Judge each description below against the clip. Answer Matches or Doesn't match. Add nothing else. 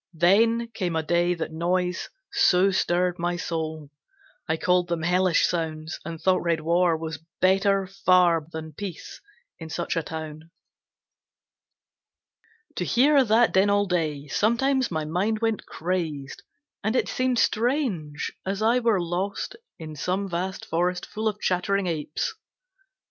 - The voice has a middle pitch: Matches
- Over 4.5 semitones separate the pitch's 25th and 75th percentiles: Doesn't match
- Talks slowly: Doesn't match